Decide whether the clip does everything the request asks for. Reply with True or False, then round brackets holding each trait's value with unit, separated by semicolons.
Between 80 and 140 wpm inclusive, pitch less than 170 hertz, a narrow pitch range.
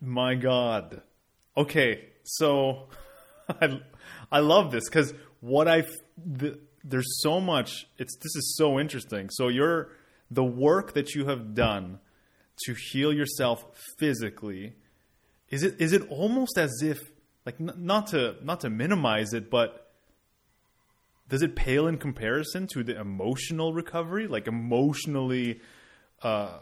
False (135 wpm; 140 Hz; 4.7 semitones)